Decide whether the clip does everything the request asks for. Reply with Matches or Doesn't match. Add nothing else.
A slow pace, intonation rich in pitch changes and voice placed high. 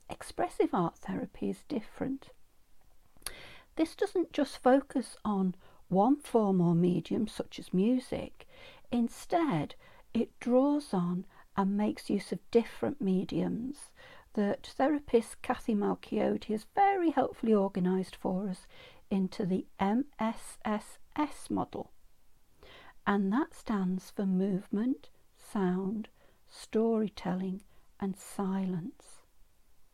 Matches